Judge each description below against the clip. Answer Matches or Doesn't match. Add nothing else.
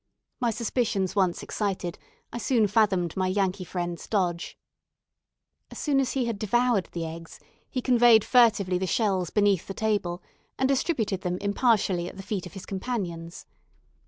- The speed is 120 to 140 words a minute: Doesn't match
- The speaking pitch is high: Matches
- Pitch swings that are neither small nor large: Matches